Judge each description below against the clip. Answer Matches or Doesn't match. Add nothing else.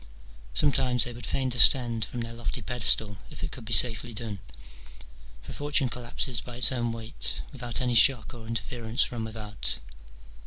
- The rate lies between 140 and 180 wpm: Matches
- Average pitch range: Doesn't match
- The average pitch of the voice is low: Matches